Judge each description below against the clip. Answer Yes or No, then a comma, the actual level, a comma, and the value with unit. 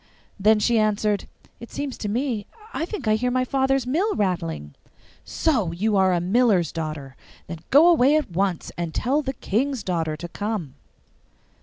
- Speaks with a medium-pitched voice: No, high, 215 Hz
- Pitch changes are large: Yes, wide, 7.0 semitones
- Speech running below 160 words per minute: No, average, 175 wpm